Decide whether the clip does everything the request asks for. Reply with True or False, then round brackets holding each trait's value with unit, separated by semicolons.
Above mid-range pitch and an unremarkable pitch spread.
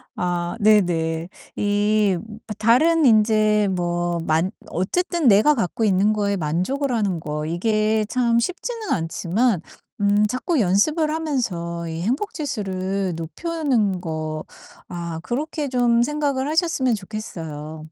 False (210 Hz; 6.6 semitones)